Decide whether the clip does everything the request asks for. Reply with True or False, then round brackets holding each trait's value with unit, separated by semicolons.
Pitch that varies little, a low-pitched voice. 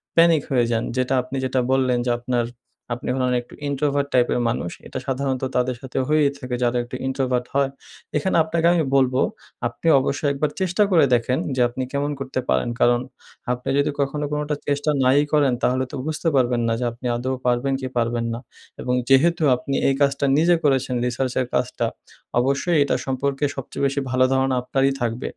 True (2.3 semitones; 130 Hz)